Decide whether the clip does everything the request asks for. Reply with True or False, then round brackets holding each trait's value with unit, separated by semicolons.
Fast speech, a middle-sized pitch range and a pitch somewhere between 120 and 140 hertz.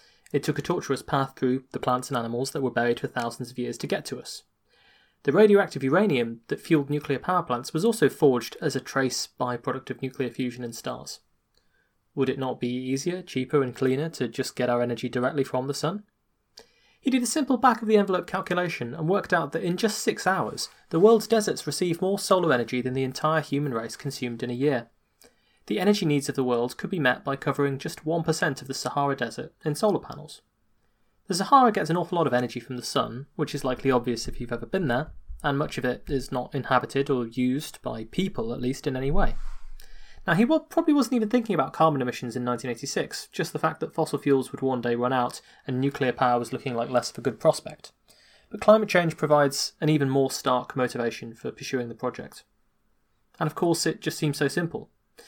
True (220 wpm; 4.7 semitones; 135 Hz)